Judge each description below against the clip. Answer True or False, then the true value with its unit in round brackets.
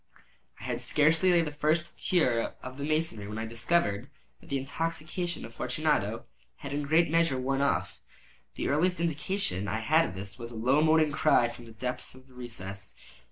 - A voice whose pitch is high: False (140 Hz)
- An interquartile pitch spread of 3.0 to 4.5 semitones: False (5.5 semitones)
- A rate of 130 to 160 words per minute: False (195 wpm)